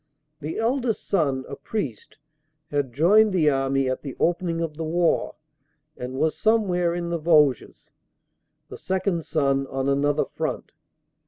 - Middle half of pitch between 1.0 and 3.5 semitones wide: No, average, 4.3 semitones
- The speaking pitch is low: No, medium, 160 Hz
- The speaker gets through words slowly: No, average, 150 wpm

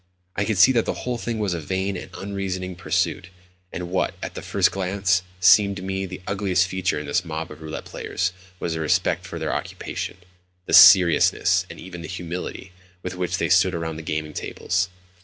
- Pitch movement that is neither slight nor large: No, narrow, 1.9 semitones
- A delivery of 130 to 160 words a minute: No, average, 195 wpm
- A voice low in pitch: Yes, very low, 90 Hz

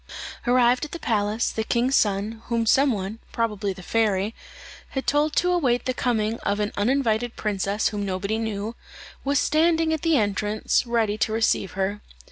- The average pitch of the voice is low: No, high, 225 Hz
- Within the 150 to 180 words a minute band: Yes, average, 170 wpm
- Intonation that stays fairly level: No, average, 3.6 semitones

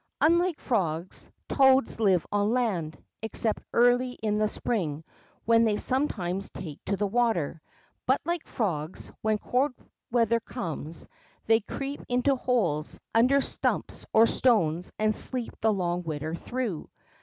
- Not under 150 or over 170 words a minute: No, slow, 135 wpm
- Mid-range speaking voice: No, high, 220 Hz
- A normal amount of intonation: No, wide, 6.0 semitones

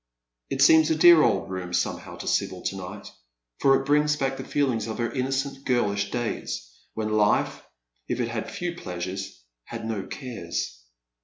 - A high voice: No, low, 120 Hz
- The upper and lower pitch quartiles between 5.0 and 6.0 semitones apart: Yes, wide, 5.5 semitones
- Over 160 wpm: Yes, average, 170 wpm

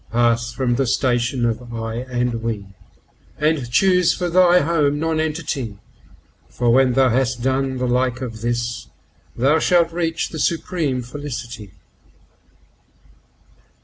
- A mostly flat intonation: No, average, 4.4 semitones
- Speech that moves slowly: Yes, slow, 120 wpm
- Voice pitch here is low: Yes, low, 130 Hz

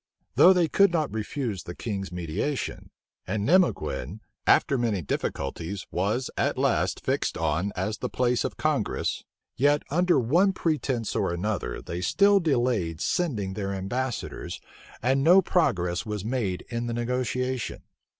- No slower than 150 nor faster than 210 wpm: No, average, 140 wpm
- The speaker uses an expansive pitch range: Yes, wide, 6.8 semitones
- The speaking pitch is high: No, low, 120 Hz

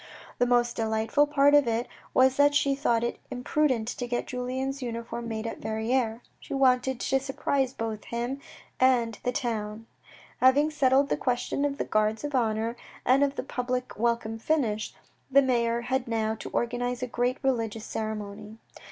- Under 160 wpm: No, average, 170 wpm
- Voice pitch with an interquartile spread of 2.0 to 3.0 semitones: Yes, average, 2.7 semitones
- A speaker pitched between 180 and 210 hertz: No, high, 245 Hz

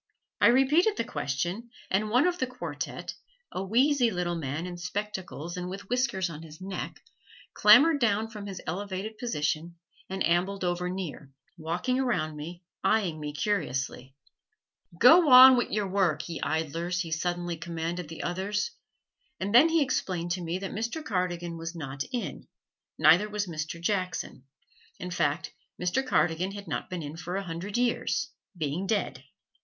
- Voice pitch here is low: No, medium, 180 Hz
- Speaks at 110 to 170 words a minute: Yes, average, 160 wpm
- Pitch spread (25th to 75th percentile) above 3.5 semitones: Yes, average, 4.4 semitones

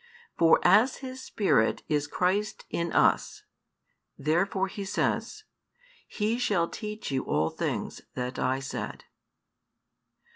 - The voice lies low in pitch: No, high, 190 Hz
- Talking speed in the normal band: No, slow, 115 wpm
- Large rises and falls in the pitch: Yes, wide, 6.4 semitones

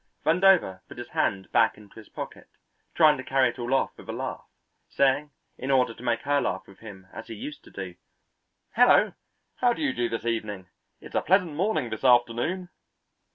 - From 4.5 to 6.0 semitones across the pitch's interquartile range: Yes, average, 5.2 semitones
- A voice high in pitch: No, low, 125 Hz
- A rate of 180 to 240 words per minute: Yes, average, 200 wpm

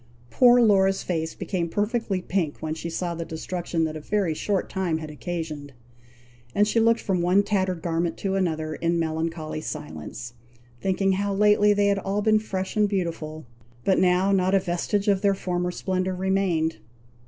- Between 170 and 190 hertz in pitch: Yes, medium, 185 Hz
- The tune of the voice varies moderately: Yes, average, 3.3 semitones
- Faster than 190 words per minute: No, average, 175 wpm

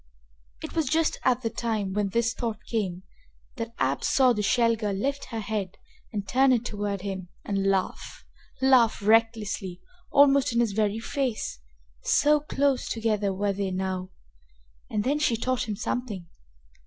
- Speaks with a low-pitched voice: No, high, 220 Hz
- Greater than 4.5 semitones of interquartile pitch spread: No, average, 3.9 semitones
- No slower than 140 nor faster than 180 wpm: Yes, average, 160 wpm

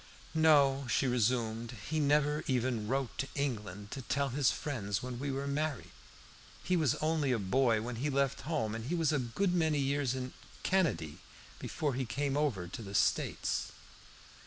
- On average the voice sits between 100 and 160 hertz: Yes, low, 135 Hz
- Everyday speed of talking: Yes, average, 175 wpm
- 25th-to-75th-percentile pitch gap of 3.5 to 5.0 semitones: Yes, average, 3.9 semitones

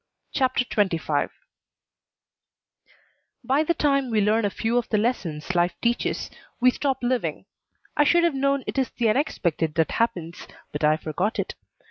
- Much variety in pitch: Yes, wide, 7.3 semitones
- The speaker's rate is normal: Yes, average, 155 wpm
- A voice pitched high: Yes, high, 230 Hz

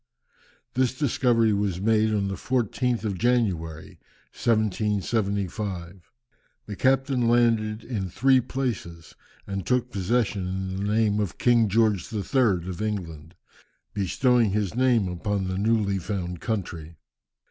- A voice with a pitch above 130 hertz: No, low, 105 Hz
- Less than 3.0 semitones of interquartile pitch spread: No, average, 3.9 semitones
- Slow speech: Yes, slow, 125 wpm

